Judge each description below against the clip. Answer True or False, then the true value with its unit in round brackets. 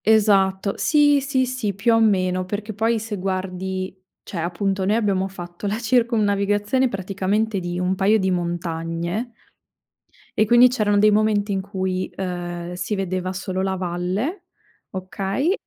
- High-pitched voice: True (195 Hz)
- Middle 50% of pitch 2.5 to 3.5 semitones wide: True (2.8 semitones)